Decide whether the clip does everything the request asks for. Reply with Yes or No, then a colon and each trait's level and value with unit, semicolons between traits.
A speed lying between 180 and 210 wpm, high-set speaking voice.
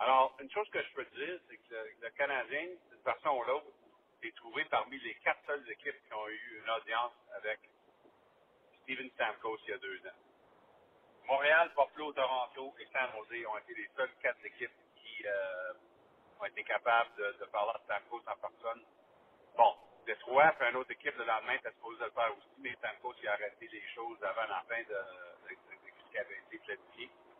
Yes: average, 195 wpm; very high, 285 Hz